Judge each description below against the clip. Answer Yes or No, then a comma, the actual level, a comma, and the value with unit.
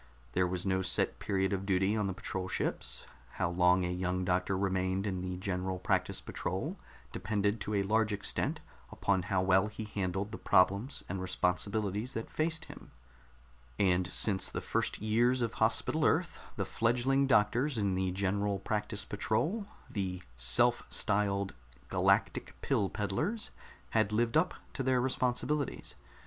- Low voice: Yes, low, 100 Hz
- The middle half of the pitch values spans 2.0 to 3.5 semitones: Yes, average, 3.2 semitones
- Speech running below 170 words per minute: Yes, average, 155 wpm